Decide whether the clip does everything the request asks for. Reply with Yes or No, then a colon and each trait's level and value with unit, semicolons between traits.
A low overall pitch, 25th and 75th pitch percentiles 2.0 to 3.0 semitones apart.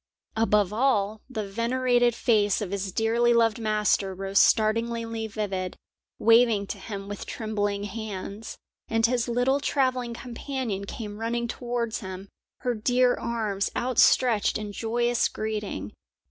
No: high, 225 Hz; average, 2.7 semitones